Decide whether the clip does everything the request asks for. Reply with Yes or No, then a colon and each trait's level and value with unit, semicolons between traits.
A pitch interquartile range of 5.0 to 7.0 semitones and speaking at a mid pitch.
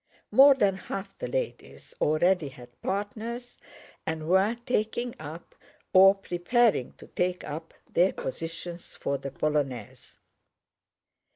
Yes: wide, 5.4 semitones; medium, 180 Hz